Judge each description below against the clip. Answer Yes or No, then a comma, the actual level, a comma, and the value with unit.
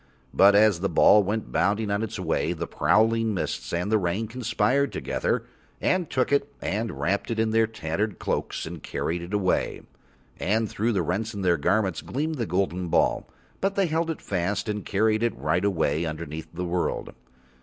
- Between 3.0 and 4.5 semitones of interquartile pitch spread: Yes, average, 4.2 semitones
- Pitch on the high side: No, low, 105 Hz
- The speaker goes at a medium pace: Yes, average, 190 wpm